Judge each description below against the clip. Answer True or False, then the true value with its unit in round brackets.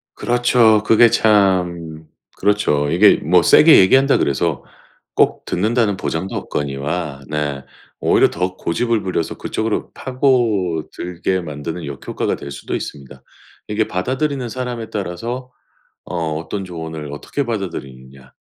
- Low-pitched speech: True (90 Hz)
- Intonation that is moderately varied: False (6.4 semitones)